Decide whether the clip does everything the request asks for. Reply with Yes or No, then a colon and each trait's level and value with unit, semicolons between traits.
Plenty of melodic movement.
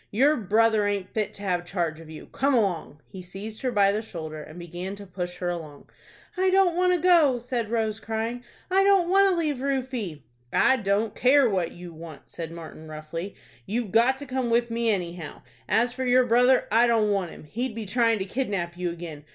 Yes: wide, 6.0 semitones